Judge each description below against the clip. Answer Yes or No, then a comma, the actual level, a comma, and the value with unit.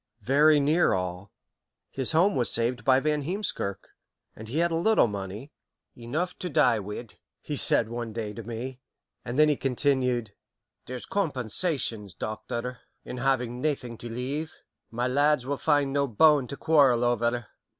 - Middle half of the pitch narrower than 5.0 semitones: Yes, average, 4.1 semitones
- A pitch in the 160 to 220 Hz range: No, low, 125 Hz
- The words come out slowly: No, average, 160 wpm